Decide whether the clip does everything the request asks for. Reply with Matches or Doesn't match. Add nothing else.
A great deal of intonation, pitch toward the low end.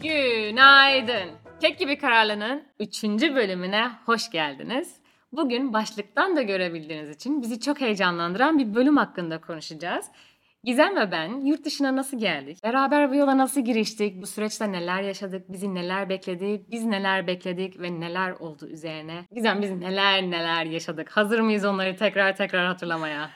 Doesn't match